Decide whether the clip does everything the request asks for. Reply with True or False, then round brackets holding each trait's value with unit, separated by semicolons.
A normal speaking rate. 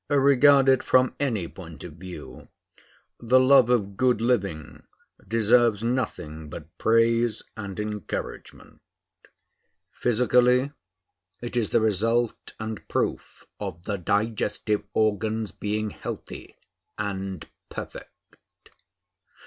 False (100 wpm)